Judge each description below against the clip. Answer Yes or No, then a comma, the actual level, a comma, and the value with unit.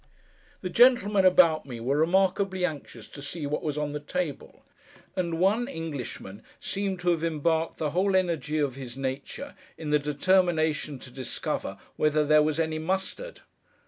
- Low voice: No, medium, 160 Hz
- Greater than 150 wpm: Yes, average, 160 wpm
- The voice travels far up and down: No, average, 4.1 semitones